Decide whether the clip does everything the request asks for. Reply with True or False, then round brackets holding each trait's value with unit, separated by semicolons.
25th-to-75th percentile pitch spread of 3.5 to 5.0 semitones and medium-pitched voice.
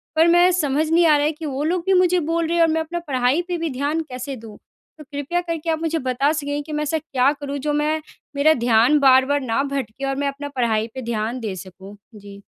False (3.9 semitones; 285 Hz)